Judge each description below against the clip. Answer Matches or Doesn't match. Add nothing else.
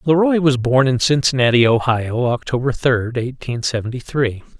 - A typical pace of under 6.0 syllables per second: Matches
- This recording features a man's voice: Matches